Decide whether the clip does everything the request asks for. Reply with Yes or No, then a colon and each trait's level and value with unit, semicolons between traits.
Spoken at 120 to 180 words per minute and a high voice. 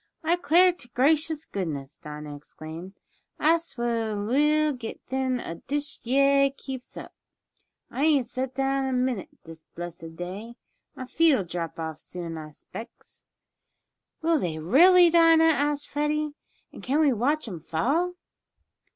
Yes: average, 140 wpm; very high, 260 Hz